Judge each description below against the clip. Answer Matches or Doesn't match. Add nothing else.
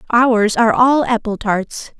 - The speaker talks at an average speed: Matches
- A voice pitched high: Matches